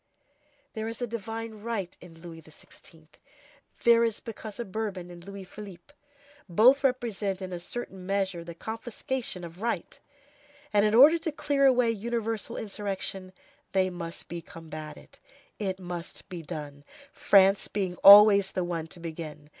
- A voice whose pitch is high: Yes, high, 195 Hz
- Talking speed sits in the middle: Yes, average, 150 wpm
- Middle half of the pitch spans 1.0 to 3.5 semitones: No, average, 4.6 semitones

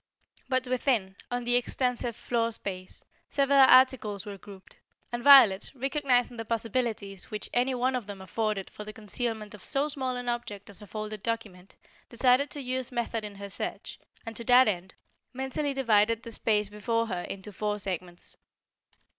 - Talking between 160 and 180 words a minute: Yes, average, 170 wpm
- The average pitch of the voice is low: No, high, 230 Hz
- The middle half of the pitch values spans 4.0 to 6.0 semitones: No, average, 3.5 semitones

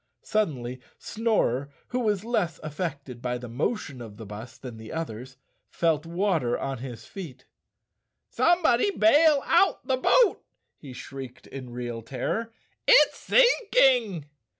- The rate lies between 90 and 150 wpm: Yes, slow, 135 wpm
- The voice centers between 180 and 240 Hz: No, medium, 155 Hz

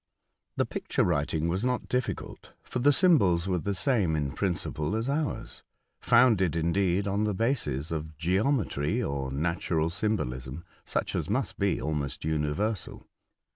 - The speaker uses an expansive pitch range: Yes, wide, 6.1 semitones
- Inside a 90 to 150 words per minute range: Yes, average, 140 wpm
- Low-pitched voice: Yes, very low, 90 Hz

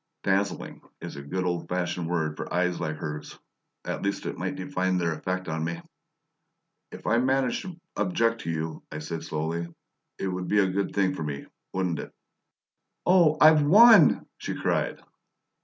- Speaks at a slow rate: No, average, 175 wpm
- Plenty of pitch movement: Yes, wide, 6.0 semitones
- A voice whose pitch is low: Yes, very low, 90 Hz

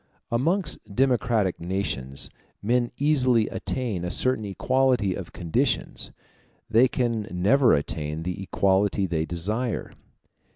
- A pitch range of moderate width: No, wide, 5.8 semitones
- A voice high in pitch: No, low, 105 Hz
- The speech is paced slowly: Yes, slow, 110 wpm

